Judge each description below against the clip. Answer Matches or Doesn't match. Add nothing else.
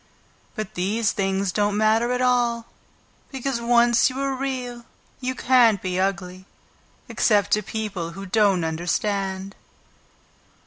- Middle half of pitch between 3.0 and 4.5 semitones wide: Matches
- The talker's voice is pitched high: Matches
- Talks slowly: Matches